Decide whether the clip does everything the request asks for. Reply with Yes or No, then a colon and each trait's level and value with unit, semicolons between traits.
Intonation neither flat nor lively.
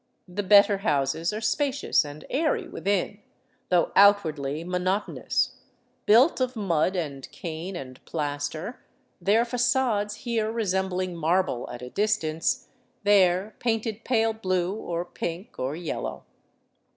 Yes: average, 5.0 semitones